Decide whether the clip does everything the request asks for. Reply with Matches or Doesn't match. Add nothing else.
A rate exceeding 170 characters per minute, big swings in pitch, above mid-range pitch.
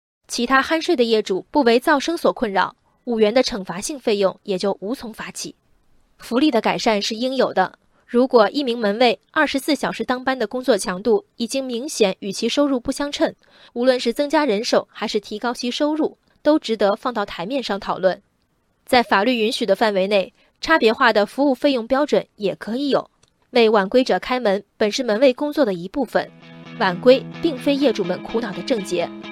Doesn't match